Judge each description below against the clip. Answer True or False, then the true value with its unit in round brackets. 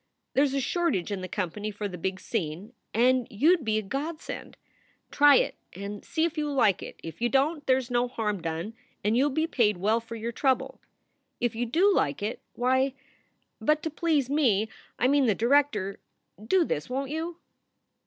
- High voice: True (245 Hz)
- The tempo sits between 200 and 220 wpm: True (205 wpm)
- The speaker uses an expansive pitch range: True (5.7 semitones)